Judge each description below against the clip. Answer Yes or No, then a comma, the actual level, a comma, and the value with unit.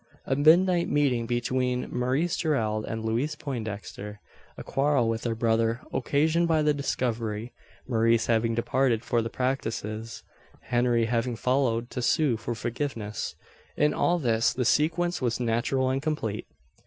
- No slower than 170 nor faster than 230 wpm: No, average, 140 wpm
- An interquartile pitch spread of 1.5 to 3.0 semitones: No, average, 3.7 semitones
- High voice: No, low, 120 Hz